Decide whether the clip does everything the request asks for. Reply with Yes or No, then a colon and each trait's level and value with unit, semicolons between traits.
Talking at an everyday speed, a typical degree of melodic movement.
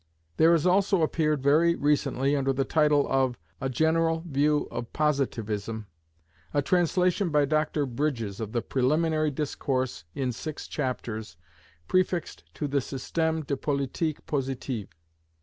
No: slow, 130 wpm; average, 3.4 semitones